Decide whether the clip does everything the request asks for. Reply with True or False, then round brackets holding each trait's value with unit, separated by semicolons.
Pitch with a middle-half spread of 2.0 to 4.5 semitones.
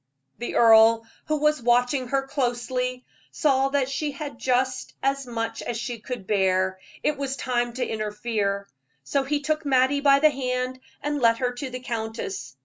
True (3.1 semitones)